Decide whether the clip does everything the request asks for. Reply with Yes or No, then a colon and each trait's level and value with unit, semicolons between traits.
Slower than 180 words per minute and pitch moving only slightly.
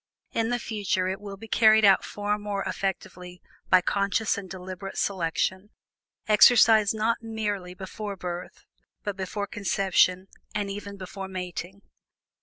Yes: slow, 135 wpm; narrow, 2.0 semitones